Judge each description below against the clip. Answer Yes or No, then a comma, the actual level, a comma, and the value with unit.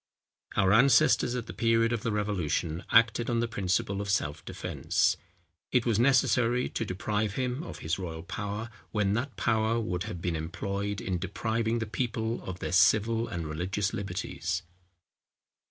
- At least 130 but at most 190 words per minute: Yes, average, 160 wpm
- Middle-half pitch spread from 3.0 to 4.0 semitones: Yes, average, 3.7 semitones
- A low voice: Yes, low, 105 Hz